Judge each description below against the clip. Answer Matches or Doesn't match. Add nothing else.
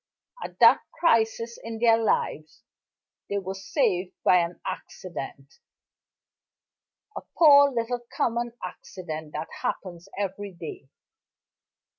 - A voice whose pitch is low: Doesn't match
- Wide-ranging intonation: Doesn't match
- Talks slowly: Matches